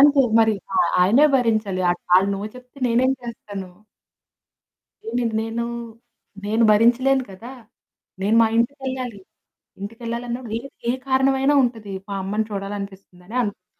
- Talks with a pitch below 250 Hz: Yes, high, 230 Hz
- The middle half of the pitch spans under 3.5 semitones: No, average, 3.8 semitones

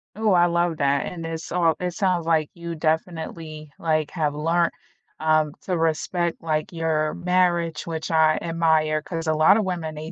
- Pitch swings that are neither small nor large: No, narrow, 1.7 semitones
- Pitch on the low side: No, medium, 165 Hz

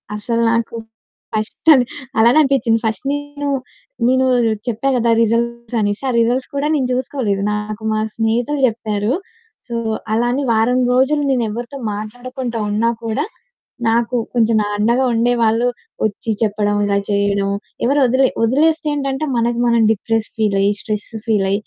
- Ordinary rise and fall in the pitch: Yes, average, 3.0 semitones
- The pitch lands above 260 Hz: No, high, 235 Hz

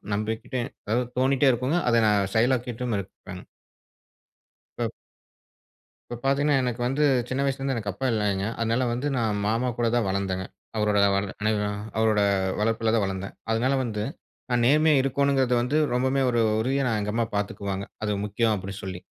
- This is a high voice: No, low, 115 Hz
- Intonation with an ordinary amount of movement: Yes, average, 3.8 semitones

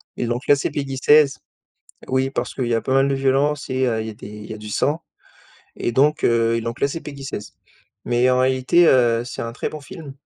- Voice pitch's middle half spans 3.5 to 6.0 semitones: No, average, 3.0 semitones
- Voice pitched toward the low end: Yes, low, 130 Hz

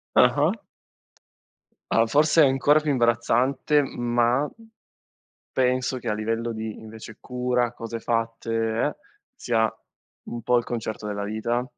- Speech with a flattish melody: Yes, narrow, 2.0 semitones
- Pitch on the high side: No, low, 120 Hz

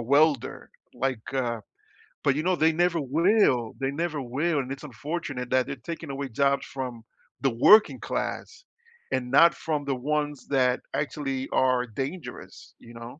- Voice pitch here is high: No, medium, 140 Hz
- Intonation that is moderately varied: Yes, average, 3.4 semitones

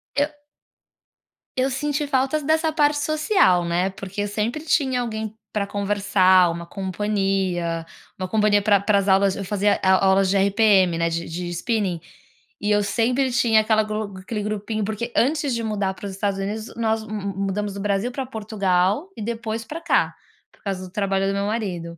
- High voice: Yes, high, 205 Hz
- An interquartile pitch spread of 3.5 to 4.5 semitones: No, average, 3.0 semitones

